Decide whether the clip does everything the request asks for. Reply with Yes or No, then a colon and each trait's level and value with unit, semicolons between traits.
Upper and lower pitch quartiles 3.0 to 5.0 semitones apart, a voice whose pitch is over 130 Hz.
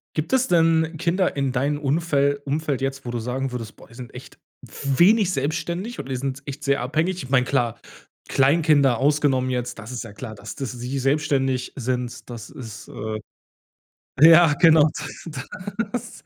Yes: average, 4.0 semitones; medium, 140 Hz